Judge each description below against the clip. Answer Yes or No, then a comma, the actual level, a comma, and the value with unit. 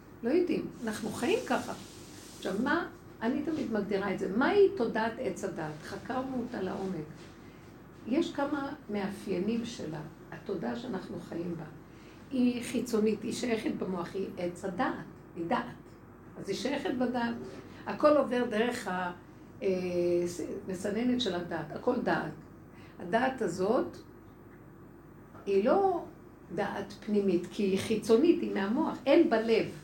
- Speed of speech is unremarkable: Yes, average, 125 wpm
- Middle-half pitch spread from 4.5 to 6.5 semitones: Yes, average, 5.1 semitones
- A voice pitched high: Yes, high, 215 Hz